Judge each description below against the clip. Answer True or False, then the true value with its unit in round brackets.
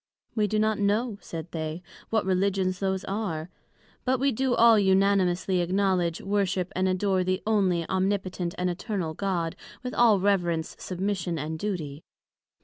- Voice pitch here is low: False (190 Hz)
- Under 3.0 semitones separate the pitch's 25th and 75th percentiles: True (2.6 semitones)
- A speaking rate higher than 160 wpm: False (145 wpm)